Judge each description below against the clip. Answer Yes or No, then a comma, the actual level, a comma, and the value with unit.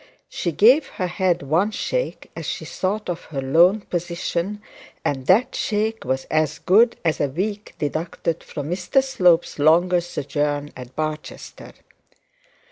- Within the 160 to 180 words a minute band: No, average, 140 wpm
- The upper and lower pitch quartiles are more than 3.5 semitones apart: Yes, average, 5.2 semitones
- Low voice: No, medium, 175 Hz